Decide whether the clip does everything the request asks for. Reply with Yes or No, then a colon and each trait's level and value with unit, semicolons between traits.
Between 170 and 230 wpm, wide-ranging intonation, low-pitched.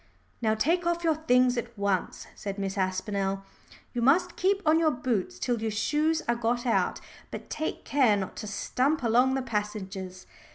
No: average, 175 wpm; wide, 6.4 semitones; high, 235 Hz